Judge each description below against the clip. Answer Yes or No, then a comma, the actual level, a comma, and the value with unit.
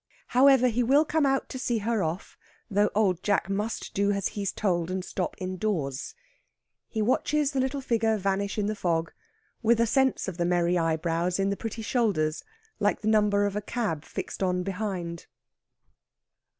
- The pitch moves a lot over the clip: No, average, 4.1 semitones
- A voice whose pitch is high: Yes, high, 205 Hz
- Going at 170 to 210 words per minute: Yes, average, 175 wpm